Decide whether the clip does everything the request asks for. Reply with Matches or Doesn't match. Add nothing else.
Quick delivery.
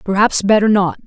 Doesn't match